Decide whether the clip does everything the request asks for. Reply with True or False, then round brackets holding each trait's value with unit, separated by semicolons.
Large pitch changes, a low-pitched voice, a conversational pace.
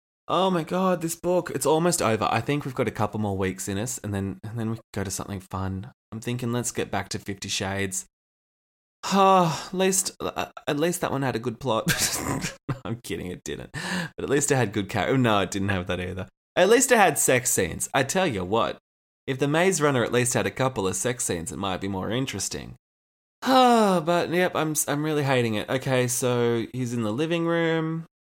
False (8.1 semitones; 120 Hz; 225 wpm)